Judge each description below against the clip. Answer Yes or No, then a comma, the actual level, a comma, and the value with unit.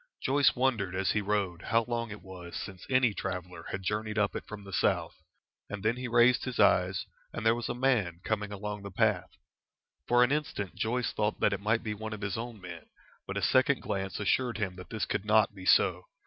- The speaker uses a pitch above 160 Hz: No, low, 105 Hz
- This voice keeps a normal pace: No, fast, 220 wpm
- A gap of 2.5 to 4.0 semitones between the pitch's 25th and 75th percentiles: Yes, average, 3.3 semitones